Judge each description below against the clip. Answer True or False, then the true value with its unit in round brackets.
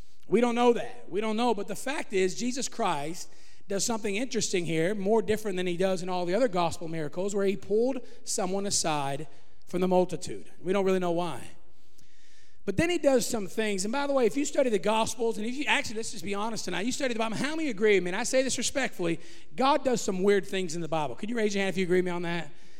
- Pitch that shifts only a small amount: False (4.6 semitones)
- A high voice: True (205 Hz)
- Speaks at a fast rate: True (260 wpm)